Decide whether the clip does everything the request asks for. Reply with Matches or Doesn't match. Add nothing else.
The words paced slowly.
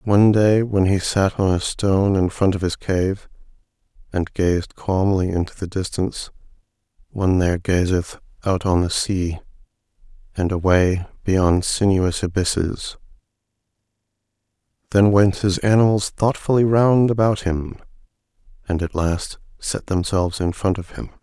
Matches